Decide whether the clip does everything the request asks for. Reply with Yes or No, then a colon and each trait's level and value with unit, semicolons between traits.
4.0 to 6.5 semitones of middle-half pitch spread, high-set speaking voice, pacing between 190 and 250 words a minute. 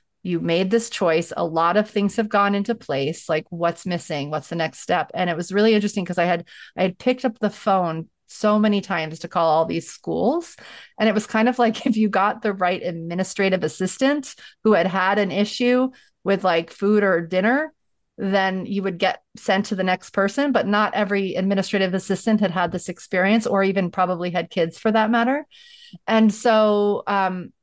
No: average, 3.3 semitones; high, 195 Hz; average, 200 wpm